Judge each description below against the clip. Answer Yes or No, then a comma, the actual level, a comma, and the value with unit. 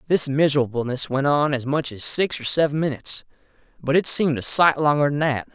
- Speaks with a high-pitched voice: No, medium, 145 Hz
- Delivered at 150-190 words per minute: No, fast, 205 wpm